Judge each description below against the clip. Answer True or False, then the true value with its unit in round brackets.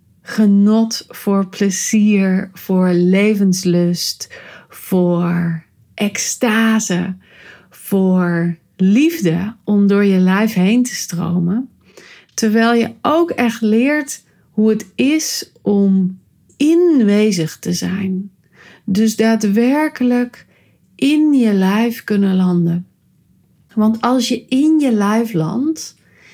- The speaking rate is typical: False (95 wpm)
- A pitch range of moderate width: True (4.2 semitones)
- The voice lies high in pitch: True (205 Hz)